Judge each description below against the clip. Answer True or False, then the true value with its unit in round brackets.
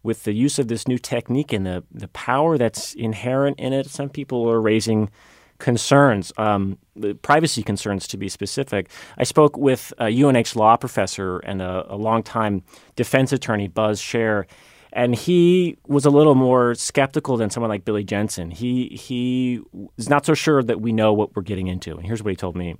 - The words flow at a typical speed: True (190 wpm)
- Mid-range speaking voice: False (115 Hz)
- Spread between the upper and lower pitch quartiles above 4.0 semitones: True (4.5 semitones)